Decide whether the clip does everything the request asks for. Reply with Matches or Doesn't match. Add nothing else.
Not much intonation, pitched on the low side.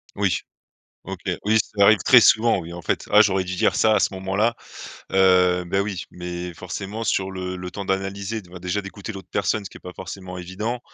Matches